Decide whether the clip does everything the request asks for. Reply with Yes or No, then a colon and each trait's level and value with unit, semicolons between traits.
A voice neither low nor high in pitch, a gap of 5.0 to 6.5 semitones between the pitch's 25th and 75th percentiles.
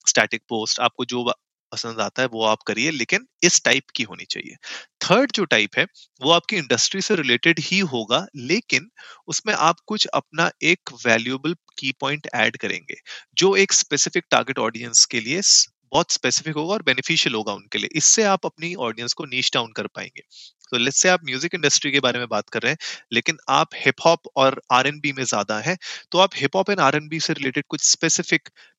Yes: medium, 145 Hz; wide, 5.5 semitones